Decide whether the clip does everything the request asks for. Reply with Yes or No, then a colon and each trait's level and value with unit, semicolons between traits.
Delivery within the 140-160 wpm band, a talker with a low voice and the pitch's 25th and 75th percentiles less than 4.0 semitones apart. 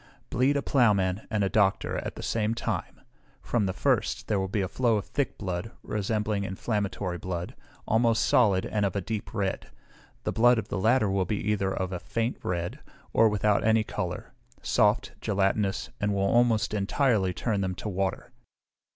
No: average, 175 wpm; low, 105 Hz; narrow, 2.6 semitones